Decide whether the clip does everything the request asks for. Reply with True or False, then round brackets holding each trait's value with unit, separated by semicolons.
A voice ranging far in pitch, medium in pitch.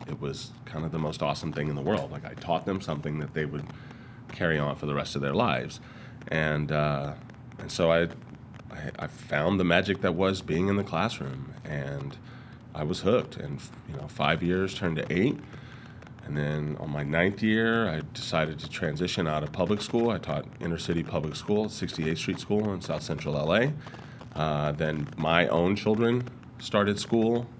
False (6.4 semitones; 85 Hz)